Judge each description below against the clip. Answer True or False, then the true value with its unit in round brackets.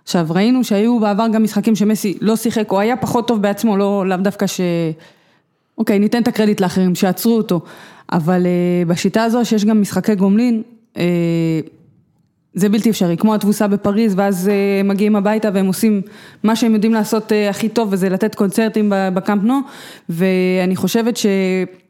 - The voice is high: True (205 Hz)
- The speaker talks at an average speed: True (155 wpm)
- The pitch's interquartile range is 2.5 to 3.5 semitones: True (3.0 semitones)